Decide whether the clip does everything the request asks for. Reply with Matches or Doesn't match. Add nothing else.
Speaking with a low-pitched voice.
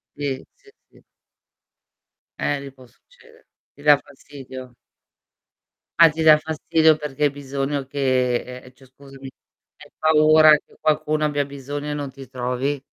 Doesn't match